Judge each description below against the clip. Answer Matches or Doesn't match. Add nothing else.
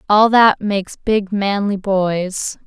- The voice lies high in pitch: Matches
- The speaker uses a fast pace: Doesn't match